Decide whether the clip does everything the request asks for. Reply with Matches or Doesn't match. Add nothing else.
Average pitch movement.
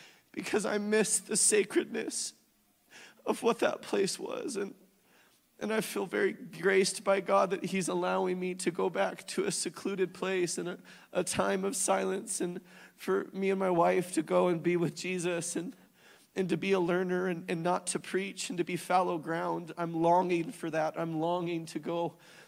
Doesn't match